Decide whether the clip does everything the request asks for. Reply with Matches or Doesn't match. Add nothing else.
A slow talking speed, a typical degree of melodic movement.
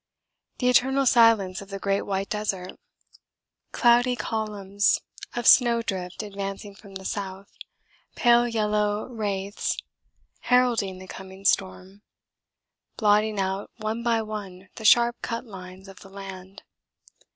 Matches